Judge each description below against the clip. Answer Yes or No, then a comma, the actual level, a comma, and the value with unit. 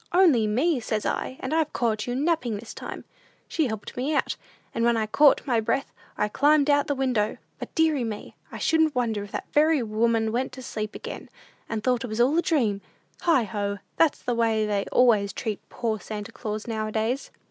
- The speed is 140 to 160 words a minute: No, fast, 205 wpm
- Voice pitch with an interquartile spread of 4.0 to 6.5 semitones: Yes, average, 4.7 semitones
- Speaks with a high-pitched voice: Yes, high, 235 Hz